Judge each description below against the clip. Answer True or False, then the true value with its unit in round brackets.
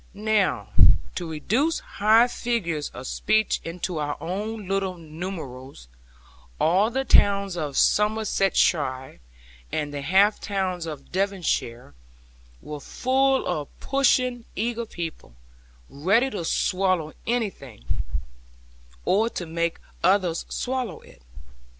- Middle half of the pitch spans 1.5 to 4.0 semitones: False (5.5 semitones)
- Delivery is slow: True (105 wpm)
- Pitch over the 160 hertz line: True (190 Hz)